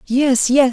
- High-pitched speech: Yes, very high, 260 Hz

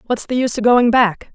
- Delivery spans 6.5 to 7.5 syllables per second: No, 6.0 syllables/s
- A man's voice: No, female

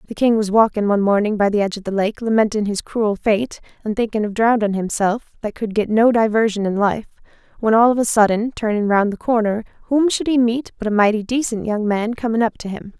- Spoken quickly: Yes, fast, 235 wpm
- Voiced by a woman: Yes, female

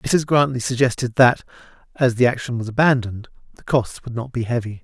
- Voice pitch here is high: No, low, 125 Hz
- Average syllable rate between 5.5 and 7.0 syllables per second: Yes, 5.7 syllables/s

